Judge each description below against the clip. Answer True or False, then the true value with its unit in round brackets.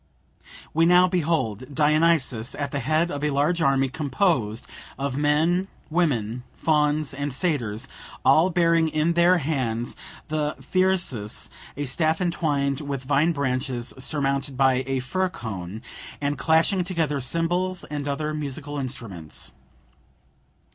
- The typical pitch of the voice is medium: True (145 Hz)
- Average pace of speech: False (125 wpm)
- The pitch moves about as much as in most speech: True (3.8 semitones)